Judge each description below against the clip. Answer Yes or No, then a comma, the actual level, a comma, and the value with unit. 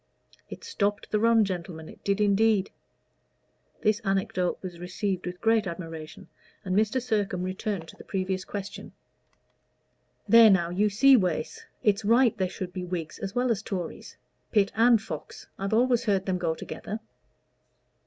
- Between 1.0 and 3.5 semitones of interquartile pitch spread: Yes, average, 3.2 semitones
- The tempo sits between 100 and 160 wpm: Yes, average, 155 wpm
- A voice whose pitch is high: Yes, high, 200 Hz